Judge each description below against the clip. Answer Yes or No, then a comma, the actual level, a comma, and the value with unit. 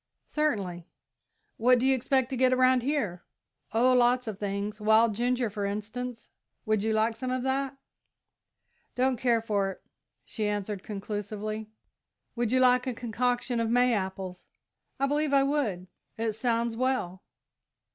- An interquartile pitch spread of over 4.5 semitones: No, average, 3.4 semitones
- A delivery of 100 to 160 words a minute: Yes, average, 150 wpm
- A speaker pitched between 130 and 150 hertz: No, high, 230 Hz